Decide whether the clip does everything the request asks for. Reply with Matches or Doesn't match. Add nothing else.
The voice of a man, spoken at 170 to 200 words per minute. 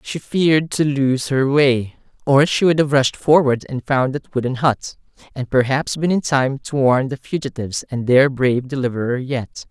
Matches